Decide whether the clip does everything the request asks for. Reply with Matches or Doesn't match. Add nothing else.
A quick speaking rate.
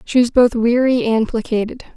Doesn't match